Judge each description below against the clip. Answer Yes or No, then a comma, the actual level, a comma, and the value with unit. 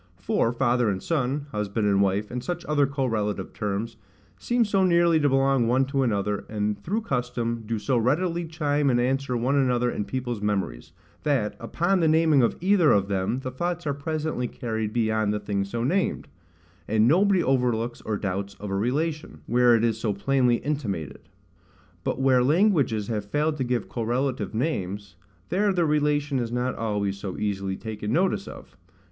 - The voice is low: Yes, low, 125 Hz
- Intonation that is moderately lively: No, wide, 5.8 semitones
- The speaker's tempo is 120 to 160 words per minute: No, average, 175 wpm